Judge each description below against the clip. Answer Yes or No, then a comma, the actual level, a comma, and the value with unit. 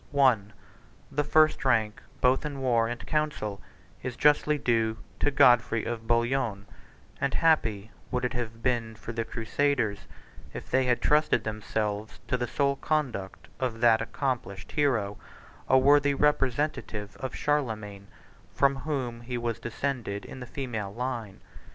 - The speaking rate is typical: Yes, average, 145 wpm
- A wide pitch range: No, average, 3.7 semitones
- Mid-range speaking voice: No, low, 120 Hz